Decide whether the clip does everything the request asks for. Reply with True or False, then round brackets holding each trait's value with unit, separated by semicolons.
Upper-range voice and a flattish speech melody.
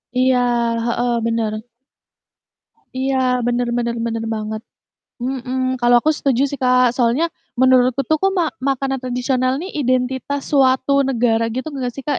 True (255 Hz; 1.8 semitones)